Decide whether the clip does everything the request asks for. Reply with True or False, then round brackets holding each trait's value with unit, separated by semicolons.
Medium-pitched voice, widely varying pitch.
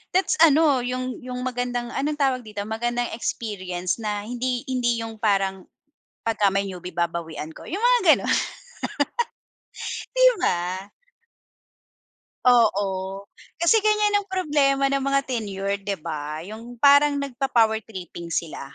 False (235 Hz; 6.0 semitones)